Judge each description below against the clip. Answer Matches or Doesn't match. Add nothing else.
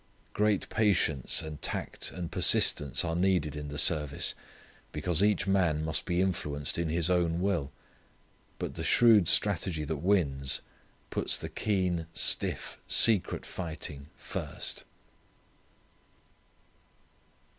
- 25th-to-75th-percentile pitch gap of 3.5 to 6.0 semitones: Matches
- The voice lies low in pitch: Matches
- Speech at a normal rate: Doesn't match